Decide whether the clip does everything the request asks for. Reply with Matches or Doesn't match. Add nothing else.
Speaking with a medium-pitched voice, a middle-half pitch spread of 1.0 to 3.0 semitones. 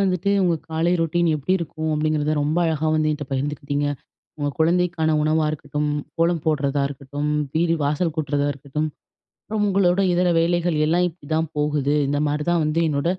Matches